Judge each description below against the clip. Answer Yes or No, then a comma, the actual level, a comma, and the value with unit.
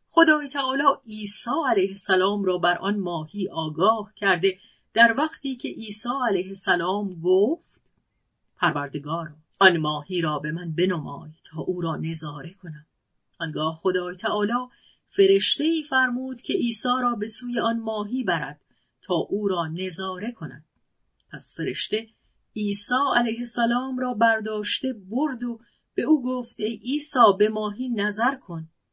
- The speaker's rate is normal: Yes, average, 140 wpm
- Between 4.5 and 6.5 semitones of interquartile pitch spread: Yes, wide, 5.6 semitones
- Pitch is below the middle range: No, high, 210 Hz